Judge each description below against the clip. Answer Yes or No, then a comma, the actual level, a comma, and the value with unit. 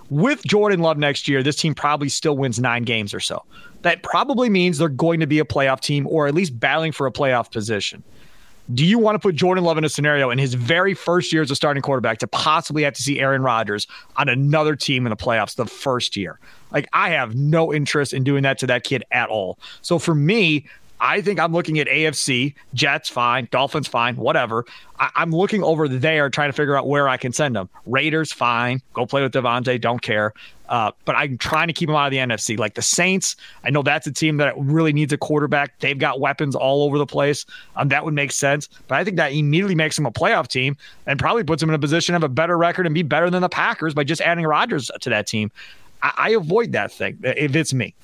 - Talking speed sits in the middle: No, fast, 240 wpm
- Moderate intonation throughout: Yes, average, 3.4 semitones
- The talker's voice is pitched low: No, medium, 145 Hz